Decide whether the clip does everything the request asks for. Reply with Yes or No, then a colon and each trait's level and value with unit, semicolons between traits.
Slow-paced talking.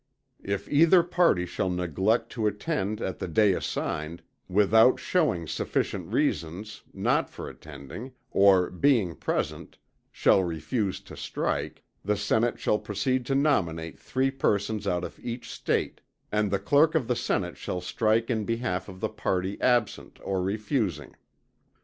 No: average, 145 wpm